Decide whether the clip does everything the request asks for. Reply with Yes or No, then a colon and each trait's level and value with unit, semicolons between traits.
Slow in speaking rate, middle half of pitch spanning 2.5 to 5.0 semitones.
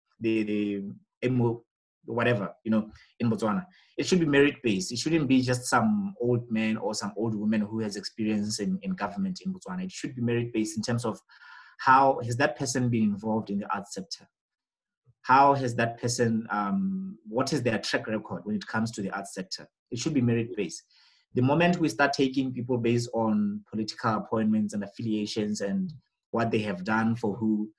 No: average, 190 wpm; average, 4.5 semitones